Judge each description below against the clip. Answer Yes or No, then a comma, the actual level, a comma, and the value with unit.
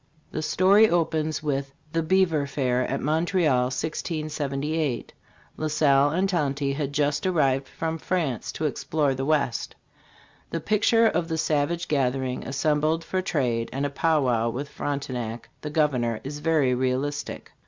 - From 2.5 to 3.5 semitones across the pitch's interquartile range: Yes, average, 3.1 semitones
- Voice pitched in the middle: Yes, medium, 145 Hz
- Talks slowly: No, average, 150 wpm